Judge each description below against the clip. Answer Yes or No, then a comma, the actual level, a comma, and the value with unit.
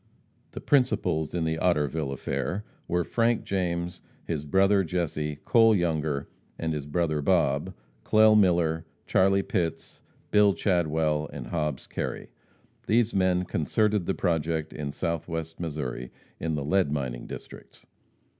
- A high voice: No, very low, 85 Hz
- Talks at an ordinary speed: No, slow, 130 wpm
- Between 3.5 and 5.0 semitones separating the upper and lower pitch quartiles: Yes, average, 3.8 semitones